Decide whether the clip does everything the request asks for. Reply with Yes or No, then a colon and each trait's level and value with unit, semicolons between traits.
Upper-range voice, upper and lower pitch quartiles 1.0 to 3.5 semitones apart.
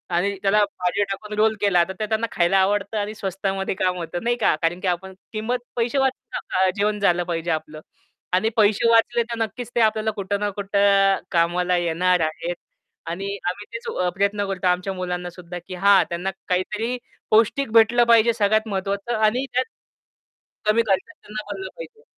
Yes: high, 200 Hz; average, 3.2 semitones